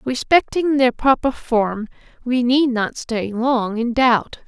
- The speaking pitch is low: No, high, 245 Hz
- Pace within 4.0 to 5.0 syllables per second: No, 3.5 syllables/s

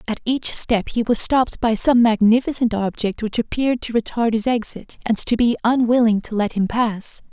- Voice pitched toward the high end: Yes, high, 230 Hz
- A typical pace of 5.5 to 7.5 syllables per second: No, 5.1 syllables/s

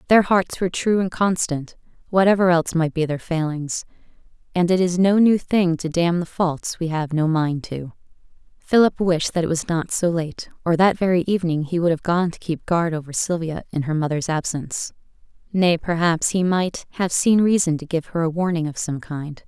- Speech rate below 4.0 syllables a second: No, 5.1 syllables/s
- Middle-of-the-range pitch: Yes, medium, 170 Hz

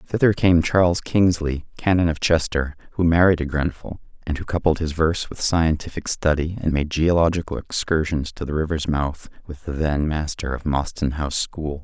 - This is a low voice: Yes, very low, 80 Hz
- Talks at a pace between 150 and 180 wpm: Yes, average, 175 wpm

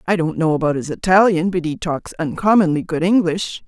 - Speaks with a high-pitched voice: No, medium, 170 Hz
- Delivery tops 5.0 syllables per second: Yes, 5.4 syllables/s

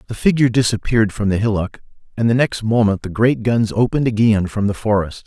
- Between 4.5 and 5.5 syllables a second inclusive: No, 6.1 syllables/s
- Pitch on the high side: No, low, 110 Hz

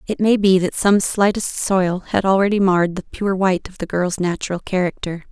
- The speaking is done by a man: No, female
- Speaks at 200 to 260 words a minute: Yes, fast, 205 wpm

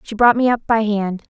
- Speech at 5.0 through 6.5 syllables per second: Yes, 5.2 syllables/s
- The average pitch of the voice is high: Yes, high, 220 Hz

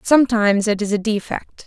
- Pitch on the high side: Yes, high, 215 Hz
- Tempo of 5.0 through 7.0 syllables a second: Yes, 5.7 syllables/s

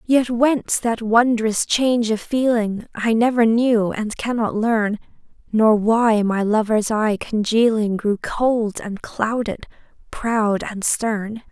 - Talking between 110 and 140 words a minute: Yes, slow, 135 wpm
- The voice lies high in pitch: Yes, high, 220 Hz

